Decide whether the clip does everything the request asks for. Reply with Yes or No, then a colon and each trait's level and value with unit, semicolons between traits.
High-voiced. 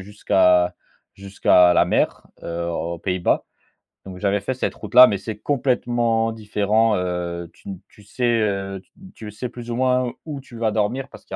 No: low, 105 Hz